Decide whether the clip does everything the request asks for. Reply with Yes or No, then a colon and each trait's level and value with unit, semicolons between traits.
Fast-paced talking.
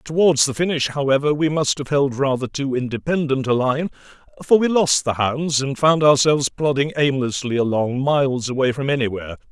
No: average, 175 wpm